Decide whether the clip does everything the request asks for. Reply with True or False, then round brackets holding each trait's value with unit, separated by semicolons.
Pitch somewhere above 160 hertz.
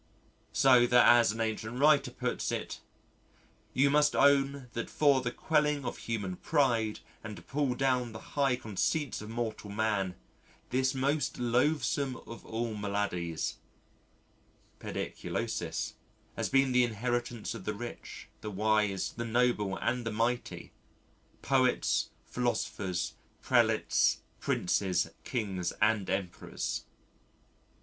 False (120 Hz)